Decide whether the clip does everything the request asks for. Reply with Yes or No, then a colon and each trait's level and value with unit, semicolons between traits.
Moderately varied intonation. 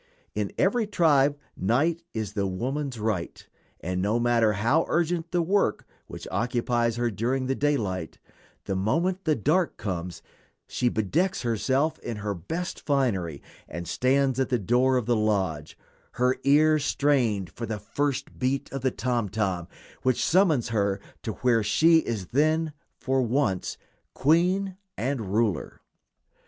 No: wide, 5.8 semitones